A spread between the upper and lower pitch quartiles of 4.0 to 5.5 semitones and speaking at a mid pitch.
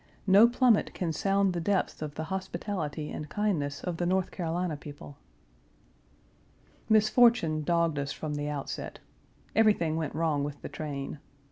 Yes: average, 4.7 semitones; medium, 165 Hz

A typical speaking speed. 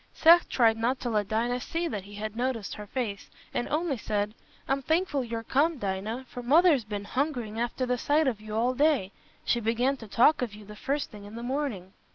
No: fast, 215 wpm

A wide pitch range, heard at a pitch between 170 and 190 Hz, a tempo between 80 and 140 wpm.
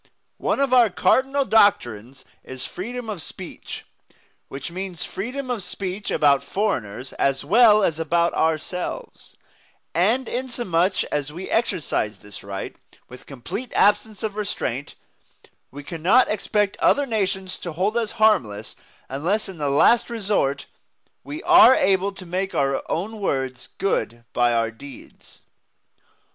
Yes: wide, 7.7 semitones; medium, 185 Hz; slow, 135 wpm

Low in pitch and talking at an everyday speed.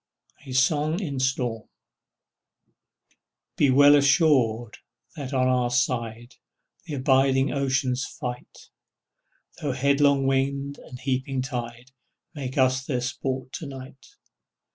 No: low, 130 Hz; slow, 110 wpm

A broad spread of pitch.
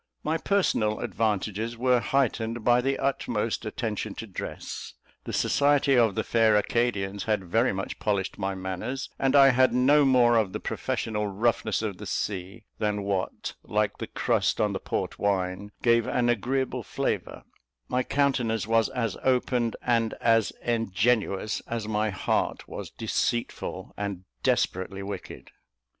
No: average, 3.3 semitones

